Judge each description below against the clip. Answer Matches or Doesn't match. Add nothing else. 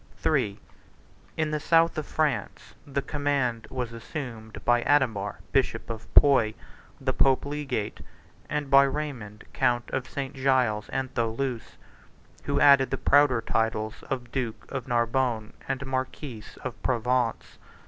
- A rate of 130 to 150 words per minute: Matches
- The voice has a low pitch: Matches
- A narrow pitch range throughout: Doesn't match